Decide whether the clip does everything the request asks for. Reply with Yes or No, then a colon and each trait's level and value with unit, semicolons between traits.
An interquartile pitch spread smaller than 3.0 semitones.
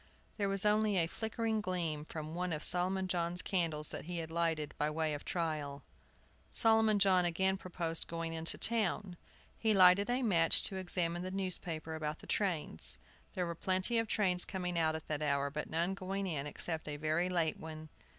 No: average, 3.3 semitones